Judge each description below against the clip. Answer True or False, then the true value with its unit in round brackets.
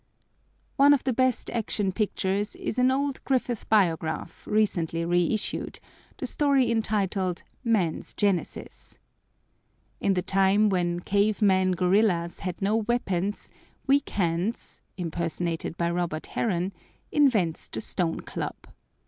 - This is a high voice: True (195 Hz)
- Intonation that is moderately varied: True (4.3 semitones)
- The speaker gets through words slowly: True (120 wpm)